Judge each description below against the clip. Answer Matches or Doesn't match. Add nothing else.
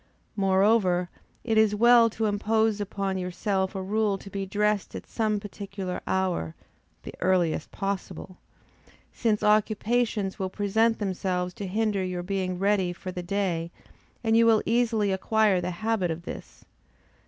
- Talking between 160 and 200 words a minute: Doesn't match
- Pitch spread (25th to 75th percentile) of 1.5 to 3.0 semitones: Matches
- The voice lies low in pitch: Doesn't match